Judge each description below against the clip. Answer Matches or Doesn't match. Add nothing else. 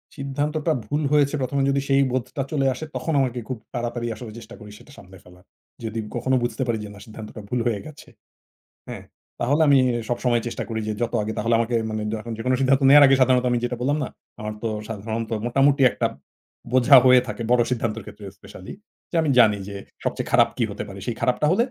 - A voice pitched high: Doesn't match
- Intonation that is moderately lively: Matches